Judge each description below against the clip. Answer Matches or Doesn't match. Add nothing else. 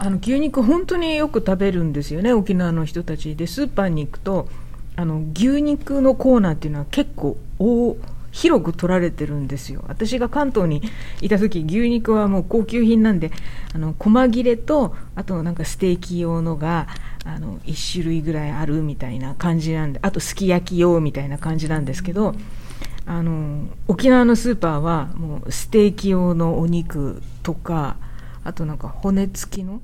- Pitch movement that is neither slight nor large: Doesn't match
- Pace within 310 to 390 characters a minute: Matches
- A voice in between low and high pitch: Matches